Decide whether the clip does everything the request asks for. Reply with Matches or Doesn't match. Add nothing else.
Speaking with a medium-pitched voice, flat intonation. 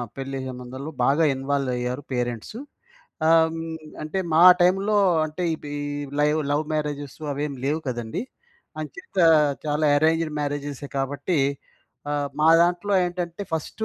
Doesn't match